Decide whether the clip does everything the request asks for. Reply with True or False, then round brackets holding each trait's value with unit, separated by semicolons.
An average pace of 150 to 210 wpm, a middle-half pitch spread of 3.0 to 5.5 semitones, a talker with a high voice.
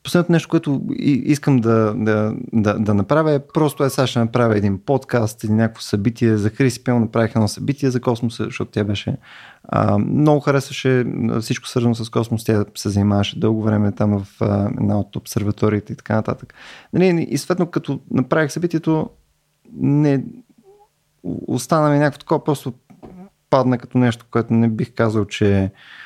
False (160 wpm; 4.7 semitones; 120 Hz)